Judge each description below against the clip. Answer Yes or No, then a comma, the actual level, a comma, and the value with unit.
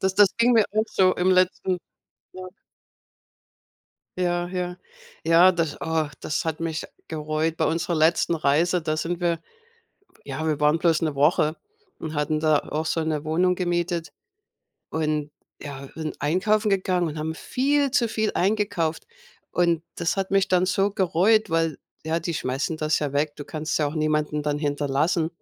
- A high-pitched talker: No, medium, 165 Hz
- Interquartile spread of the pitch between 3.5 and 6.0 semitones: No, average, 3.0 semitones